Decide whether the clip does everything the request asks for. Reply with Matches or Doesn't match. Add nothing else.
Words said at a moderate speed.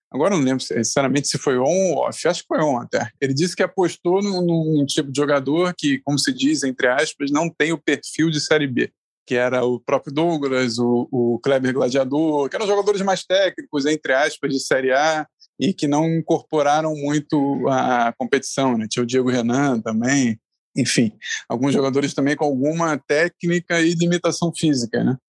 Doesn't match